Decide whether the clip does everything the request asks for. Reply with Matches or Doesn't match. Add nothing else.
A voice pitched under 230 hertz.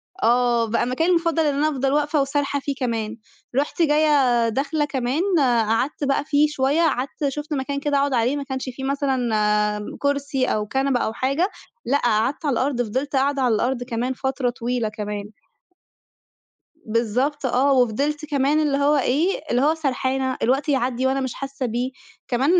Doesn't match